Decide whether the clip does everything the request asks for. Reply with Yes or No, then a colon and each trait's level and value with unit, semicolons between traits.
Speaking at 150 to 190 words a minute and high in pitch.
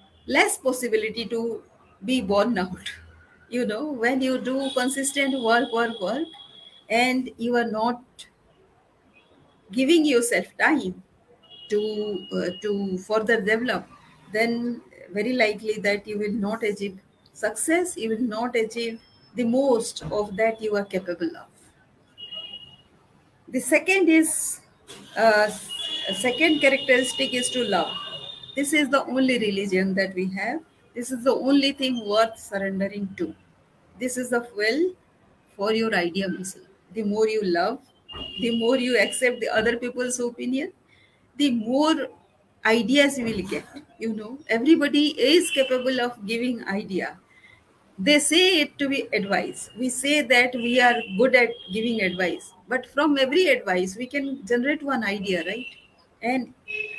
No: average, 140 wpm; high, 235 Hz